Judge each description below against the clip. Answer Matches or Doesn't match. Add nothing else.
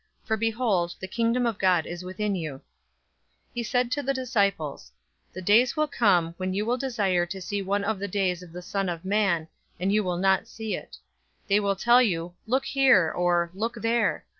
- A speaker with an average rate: Doesn't match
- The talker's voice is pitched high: Matches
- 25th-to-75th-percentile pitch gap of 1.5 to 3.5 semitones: Doesn't match